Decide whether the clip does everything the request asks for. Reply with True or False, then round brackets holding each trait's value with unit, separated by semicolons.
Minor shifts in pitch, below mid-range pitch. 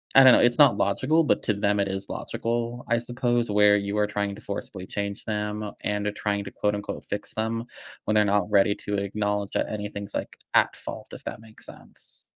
True (2.1 semitones; 105 Hz)